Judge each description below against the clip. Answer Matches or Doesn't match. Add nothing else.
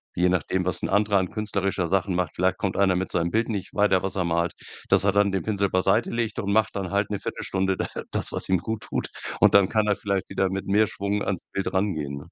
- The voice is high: Doesn't match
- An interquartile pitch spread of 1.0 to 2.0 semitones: Matches